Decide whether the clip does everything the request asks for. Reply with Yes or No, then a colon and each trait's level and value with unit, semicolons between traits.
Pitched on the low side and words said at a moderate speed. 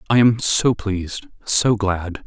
Yes: low, 100 Hz; average, 160 wpm